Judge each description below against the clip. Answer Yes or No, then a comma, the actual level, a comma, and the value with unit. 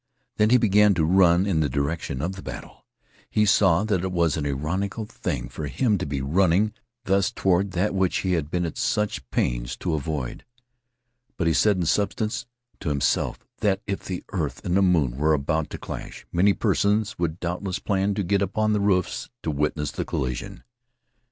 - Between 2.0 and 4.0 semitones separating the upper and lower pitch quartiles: No, average, 4.5 semitones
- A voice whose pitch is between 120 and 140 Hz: No, very low, 90 Hz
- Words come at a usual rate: Yes, average, 190 wpm